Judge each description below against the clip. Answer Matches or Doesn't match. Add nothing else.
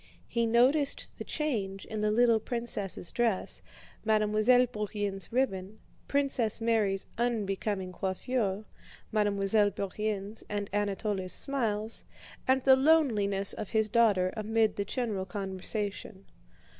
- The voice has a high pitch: Matches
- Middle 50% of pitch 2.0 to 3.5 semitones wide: Matches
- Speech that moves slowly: Matches